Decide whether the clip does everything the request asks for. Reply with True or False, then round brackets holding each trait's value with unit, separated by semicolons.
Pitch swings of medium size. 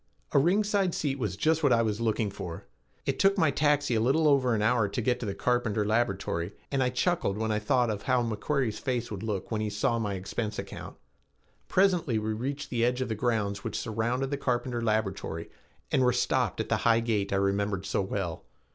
True (4.1 semitones)